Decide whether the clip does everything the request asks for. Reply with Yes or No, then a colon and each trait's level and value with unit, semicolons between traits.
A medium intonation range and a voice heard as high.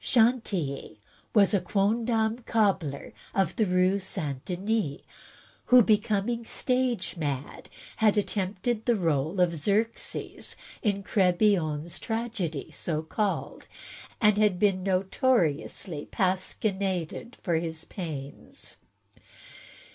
Yes: average, 4.6 semitones; high, 195 Hz